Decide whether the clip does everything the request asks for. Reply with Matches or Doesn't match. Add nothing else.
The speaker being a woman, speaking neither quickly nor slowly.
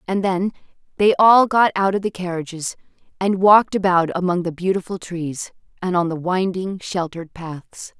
Matches